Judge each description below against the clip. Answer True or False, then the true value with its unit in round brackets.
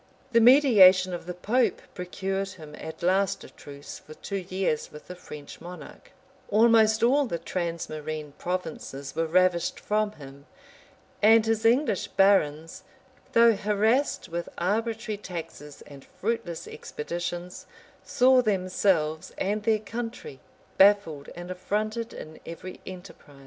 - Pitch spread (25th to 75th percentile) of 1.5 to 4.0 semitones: False (4.7 semitones)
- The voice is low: False (185 Hz)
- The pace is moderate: False (130 wpm)